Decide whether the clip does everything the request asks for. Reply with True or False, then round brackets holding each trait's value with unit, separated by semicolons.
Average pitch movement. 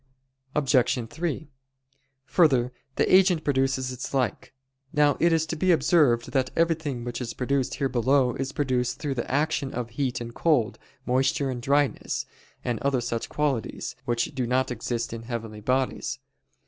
True (3.1 semitones)